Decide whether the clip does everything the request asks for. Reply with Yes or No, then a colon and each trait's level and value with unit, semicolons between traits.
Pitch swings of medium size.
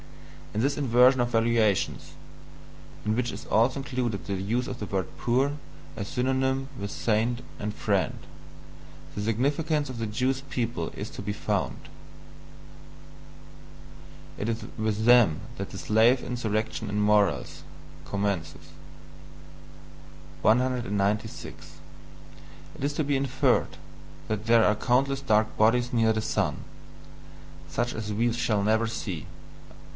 Yes: average, 3.1 semitones